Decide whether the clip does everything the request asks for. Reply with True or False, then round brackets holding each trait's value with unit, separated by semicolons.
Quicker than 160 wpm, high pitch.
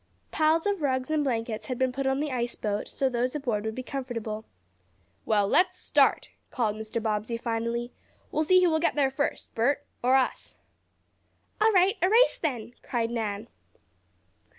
True (175 wpm; 255 Hz)